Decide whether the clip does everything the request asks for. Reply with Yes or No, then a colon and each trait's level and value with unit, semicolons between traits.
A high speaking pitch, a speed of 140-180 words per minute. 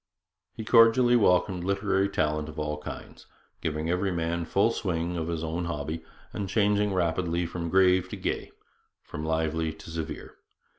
No: very low, 85 Hz; average, 155 wpm